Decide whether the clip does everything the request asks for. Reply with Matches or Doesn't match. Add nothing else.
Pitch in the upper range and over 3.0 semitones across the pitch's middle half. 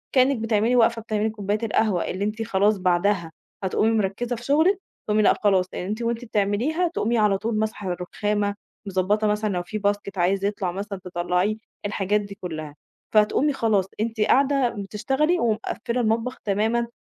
Doesn't match